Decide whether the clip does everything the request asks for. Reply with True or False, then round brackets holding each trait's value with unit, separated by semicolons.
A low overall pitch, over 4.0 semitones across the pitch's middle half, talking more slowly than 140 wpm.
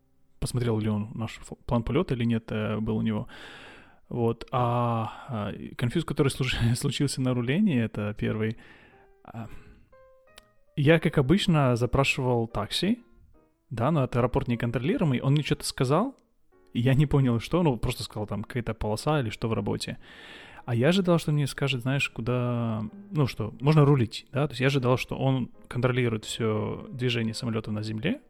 False (125 Hz; 4.5 semitones; 160 wpm)